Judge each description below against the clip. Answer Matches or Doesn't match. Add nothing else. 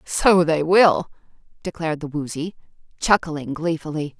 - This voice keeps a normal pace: Doesn't match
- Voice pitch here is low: Doesn't match